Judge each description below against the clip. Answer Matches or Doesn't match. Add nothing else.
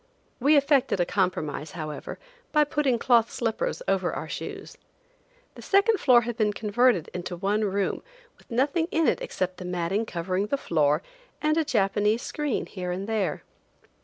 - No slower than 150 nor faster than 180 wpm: Matches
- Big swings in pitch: Matches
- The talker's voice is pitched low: Doesn't match